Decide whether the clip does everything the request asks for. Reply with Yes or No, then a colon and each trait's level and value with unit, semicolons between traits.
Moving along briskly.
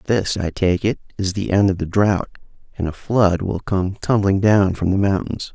Yes: fast, 215 wpm